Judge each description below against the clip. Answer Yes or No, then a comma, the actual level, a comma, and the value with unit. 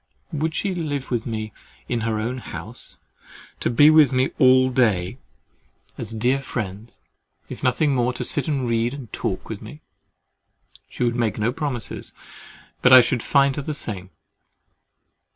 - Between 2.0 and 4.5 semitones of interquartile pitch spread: Yes, average, 3.7 semitones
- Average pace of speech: Yes, average, 150 wpm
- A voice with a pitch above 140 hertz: No, low, 125 Hz